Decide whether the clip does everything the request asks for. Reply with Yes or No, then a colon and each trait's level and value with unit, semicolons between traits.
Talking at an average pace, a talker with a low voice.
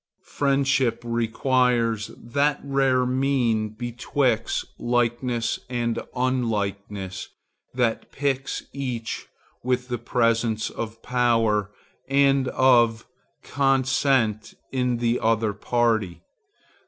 No: slow, 85 wpm; low, 120 Hz